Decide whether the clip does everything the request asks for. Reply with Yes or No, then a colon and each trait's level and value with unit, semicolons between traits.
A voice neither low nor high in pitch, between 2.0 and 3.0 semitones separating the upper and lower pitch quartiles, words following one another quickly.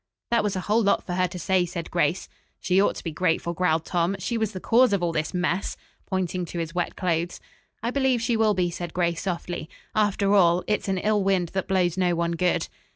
Yes: medium, 180 Hz; narrow, 2.6 semitones; fast, 230 wpm